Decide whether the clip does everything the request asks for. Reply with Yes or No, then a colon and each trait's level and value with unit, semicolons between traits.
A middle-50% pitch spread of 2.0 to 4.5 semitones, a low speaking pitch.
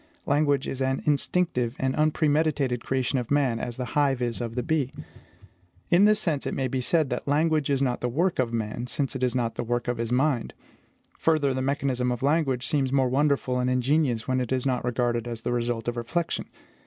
Yes: average, 2.9 semitones; low, 130 Hz